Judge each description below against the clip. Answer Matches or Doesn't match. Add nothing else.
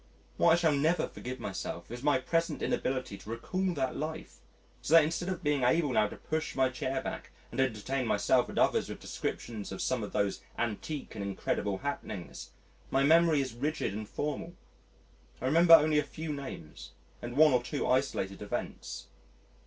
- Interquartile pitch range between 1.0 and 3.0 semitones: Doesn't match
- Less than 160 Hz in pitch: Matches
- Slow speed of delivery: Doesn't match